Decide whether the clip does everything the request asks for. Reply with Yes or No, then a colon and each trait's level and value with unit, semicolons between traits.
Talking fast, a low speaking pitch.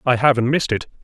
Yes: fast, 230 wpm; low, 125 Hz